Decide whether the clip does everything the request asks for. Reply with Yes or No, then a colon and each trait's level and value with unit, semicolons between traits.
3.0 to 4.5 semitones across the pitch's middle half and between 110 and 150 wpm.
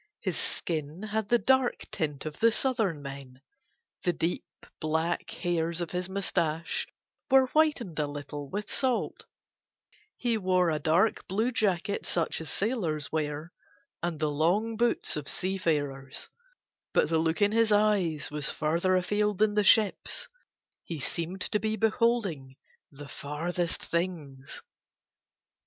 No: wide, 5.5 semitones; average, 140 wpm